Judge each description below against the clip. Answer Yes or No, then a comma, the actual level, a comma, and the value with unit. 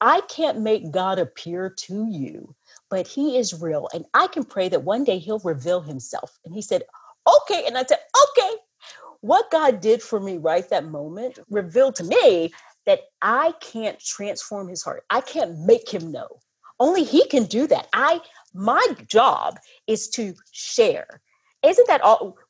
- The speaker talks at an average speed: Yes, average, 175 wpm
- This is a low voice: No, high, 225 Hz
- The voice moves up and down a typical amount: No, wide, 8.7 semitones